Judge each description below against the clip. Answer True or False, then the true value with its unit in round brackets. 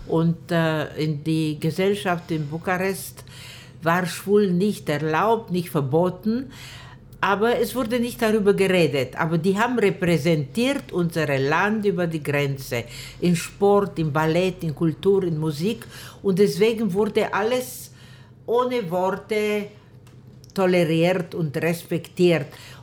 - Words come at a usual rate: False (115 wpm)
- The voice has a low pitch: False (170 Hz)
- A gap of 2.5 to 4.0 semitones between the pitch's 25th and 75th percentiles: False (4.9 semitones)